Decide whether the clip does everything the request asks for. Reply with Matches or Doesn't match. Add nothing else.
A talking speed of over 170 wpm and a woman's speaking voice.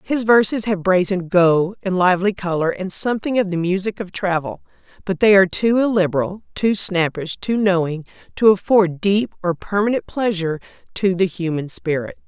Doesn't match